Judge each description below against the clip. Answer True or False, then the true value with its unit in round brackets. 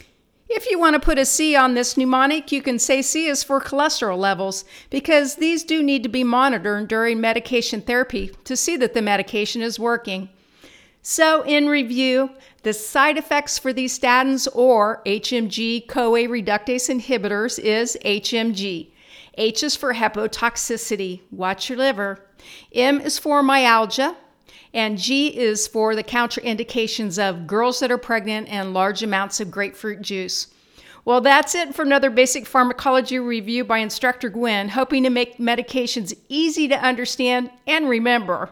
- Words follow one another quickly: False (155 wpm)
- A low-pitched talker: False (245 Hz)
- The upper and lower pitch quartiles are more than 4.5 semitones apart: False (3.6 semitones)